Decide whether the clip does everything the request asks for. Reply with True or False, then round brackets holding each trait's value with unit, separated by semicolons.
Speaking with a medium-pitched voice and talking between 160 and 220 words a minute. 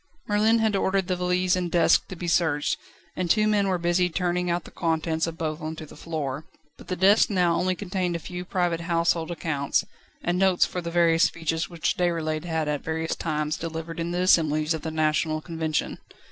True (170 Hz; 205 wpm)